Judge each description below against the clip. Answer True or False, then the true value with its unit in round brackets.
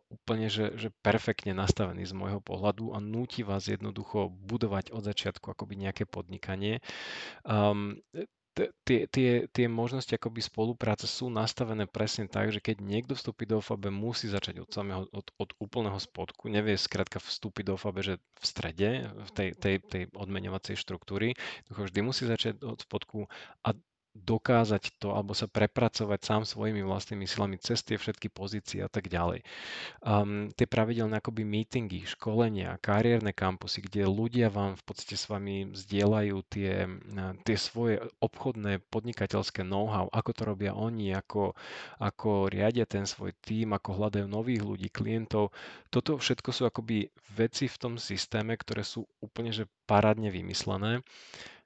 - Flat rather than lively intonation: True (2.3 semitones)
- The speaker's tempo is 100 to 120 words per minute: False (150 wpm)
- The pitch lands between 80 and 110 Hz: True (105 Hz)